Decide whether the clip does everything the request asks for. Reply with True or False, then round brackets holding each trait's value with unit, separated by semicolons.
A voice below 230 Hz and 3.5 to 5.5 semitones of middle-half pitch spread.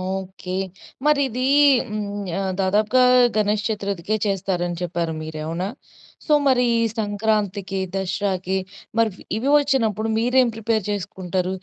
False (200 Hz; 2.8 semitones)